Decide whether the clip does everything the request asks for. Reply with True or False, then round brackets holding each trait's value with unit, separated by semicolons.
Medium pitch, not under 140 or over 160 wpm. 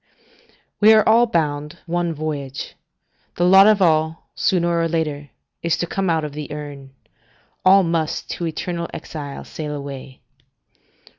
True (160 Hz; 145 wpm)